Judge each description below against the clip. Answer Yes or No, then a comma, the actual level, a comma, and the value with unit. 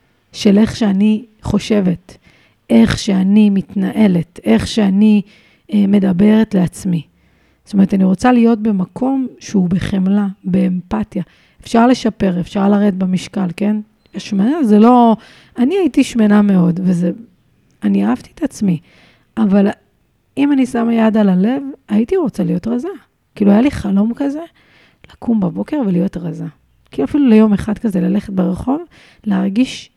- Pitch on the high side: Yes, high, 205 Hz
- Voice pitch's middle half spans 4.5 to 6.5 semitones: No, average, 3.6 semitones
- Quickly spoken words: No, average, 135 wpm